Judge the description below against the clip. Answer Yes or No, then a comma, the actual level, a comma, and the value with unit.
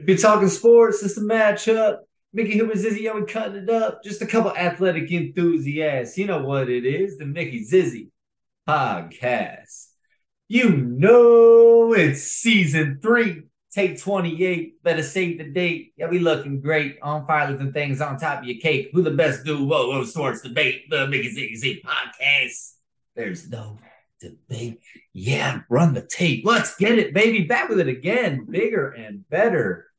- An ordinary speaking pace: Yes, average, 165 wpm